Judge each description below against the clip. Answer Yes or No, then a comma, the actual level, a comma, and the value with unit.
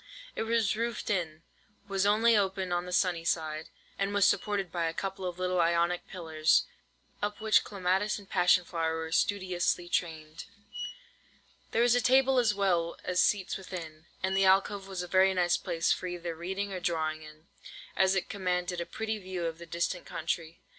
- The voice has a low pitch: No, medium, 180 Hz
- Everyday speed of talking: Yes, average, 180 wpm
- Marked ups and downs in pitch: No, average, 2.7 semitones